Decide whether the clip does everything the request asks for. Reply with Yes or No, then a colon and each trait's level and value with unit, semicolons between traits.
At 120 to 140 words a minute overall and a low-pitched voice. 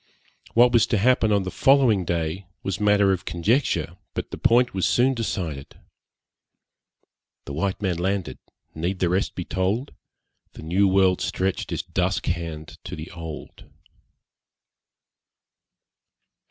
Yes: slow, 135 wpm; very low, 95 Hz